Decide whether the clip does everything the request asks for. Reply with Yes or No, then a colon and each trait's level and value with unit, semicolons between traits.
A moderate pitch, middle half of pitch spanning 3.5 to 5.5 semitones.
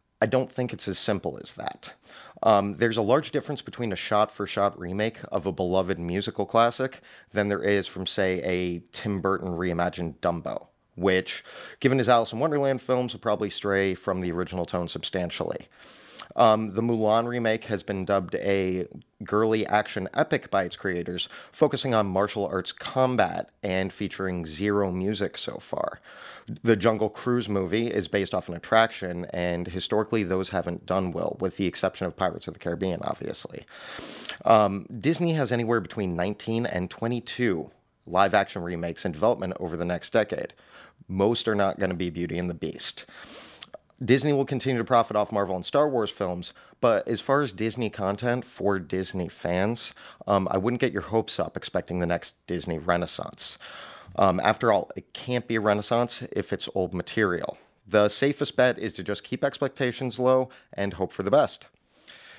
No: low, 100 Hz; average, 4.1 semitones